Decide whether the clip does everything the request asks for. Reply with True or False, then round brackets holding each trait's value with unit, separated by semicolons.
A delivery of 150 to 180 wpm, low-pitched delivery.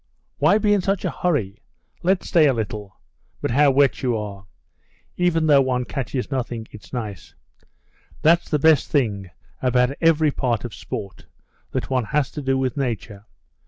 True (165 wpm; 130 Hz)